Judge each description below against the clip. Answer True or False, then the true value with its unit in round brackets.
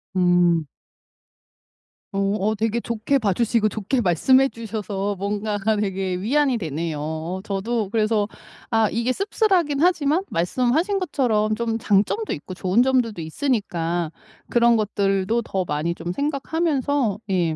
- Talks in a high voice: True (215 Hz)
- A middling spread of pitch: True (5.0 semitones)